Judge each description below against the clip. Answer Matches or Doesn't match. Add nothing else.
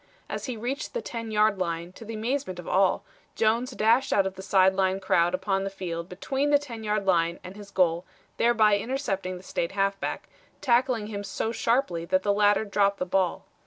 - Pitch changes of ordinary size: Matches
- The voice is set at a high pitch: Matches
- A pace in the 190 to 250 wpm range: Matches